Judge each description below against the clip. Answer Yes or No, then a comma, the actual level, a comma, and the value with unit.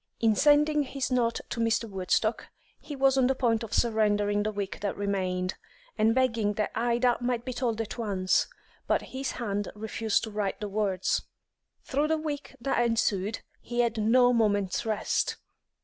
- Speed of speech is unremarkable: Yes, average, 170 wpm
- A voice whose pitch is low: No, high, 225 Hz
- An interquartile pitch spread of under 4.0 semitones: Yes, average, 3.3 semitones